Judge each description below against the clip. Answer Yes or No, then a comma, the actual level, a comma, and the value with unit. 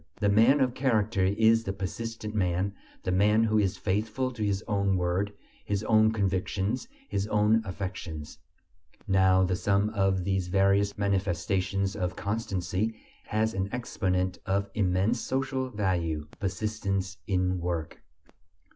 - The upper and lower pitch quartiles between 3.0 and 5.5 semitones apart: No, narrow, 2.6 semitones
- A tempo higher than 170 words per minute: No, slow, 135 wpm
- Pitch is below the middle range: Yes, low, 100 Hz